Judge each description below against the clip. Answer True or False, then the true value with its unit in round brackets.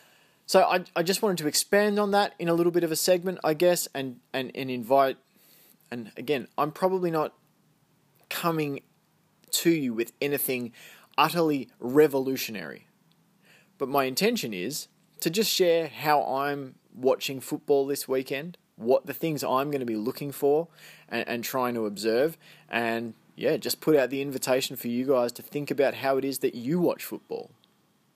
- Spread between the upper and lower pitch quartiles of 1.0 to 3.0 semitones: False (4.3 semitones)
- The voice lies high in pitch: False (145 Hz)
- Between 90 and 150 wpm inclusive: False (175 wpm)